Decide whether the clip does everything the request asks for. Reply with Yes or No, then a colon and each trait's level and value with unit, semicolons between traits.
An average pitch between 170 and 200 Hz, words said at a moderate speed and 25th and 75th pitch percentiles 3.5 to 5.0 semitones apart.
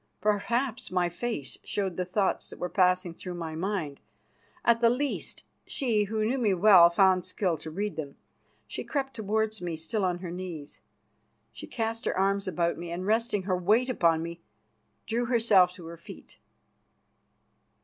Yes: high, 190 Hz; average, 170 wpm; average, 4.0 semitones